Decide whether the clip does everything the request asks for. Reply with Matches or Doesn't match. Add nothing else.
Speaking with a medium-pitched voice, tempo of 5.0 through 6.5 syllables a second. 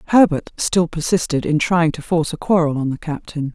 Matches